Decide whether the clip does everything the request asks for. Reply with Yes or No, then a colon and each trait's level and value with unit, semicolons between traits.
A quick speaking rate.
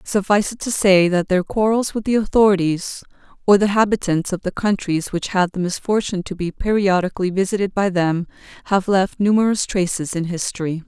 No: average, 175 wpm